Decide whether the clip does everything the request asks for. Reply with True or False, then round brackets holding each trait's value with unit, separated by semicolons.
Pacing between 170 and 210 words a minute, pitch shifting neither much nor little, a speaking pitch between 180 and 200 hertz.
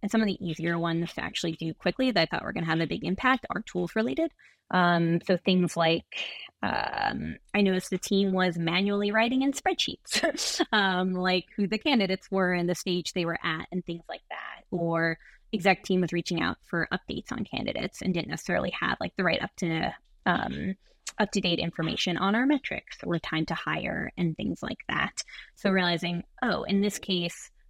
True (205 wpm; 3.2 semitones; 185 Hz)